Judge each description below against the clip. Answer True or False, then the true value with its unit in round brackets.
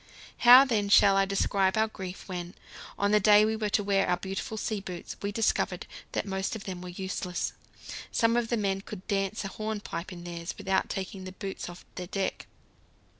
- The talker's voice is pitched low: False (195 Hz)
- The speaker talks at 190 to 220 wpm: True (200 wpm)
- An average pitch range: False (2.1 semitones)